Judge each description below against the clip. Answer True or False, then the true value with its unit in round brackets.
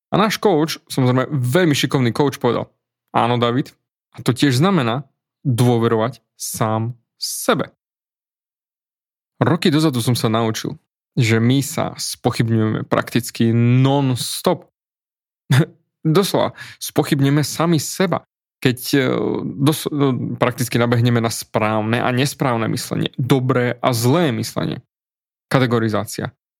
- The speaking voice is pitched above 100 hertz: True (130 Hz)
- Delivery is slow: True (105 wpm)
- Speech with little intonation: False (3.8 semitones)